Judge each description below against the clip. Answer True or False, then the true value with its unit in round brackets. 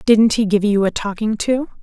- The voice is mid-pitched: False (215 Hz)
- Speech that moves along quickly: True (230 wpm)